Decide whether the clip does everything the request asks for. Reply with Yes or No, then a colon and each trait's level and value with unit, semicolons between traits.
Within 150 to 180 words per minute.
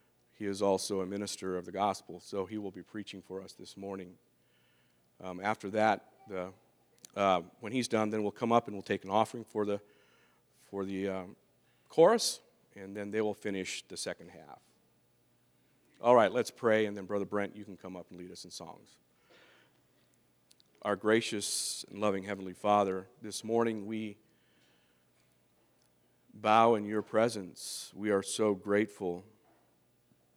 Yes: average, 160 wpm